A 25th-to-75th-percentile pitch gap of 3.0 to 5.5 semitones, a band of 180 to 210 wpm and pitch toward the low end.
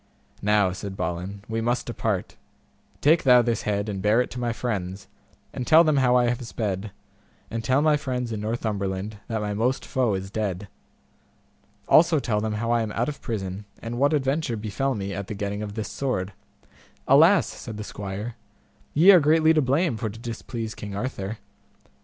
Yes: average, 3.7 semitones; average, 190 wpm; low, 110 Hz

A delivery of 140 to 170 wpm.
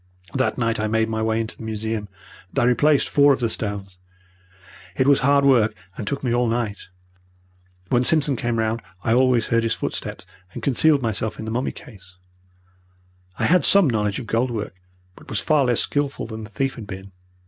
No: average, 200 wpm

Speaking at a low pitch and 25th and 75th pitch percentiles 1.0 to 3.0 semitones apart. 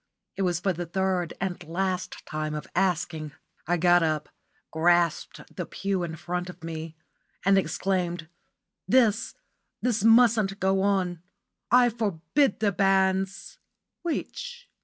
No: medium, 185 Hz; narrow, 2.6 semitones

